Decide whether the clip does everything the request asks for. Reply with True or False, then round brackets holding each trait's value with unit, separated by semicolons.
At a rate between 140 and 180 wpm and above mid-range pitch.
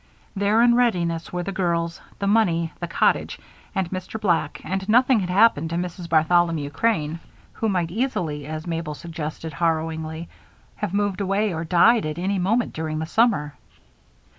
False (165 wpm; 175 Hz)